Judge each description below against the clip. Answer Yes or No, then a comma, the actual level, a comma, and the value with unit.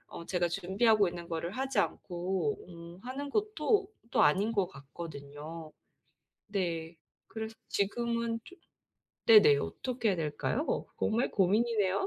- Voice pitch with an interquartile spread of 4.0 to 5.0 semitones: No, wide, 5.5 semitones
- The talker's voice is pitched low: No, high, 195 Hz